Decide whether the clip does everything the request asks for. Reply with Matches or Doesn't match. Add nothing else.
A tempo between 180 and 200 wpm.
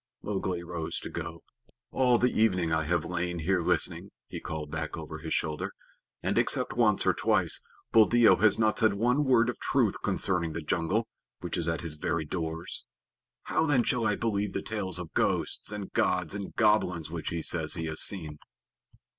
Matches